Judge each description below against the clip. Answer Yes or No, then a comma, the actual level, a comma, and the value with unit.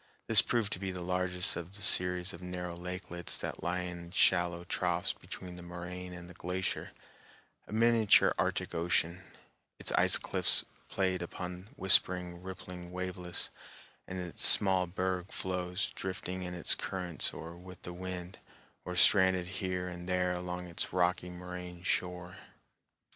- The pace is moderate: Yes, average, 155 wpm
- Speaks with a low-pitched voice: Yes, very low, 90 Hz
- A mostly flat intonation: Yes, narrow, 0.9 semitones